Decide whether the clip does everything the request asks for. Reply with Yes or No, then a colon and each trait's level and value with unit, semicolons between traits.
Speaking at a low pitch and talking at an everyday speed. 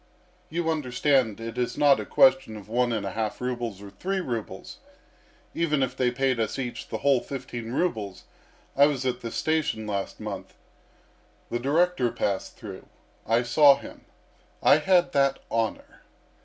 Yes: low, 125 Hz; average, 160 wpm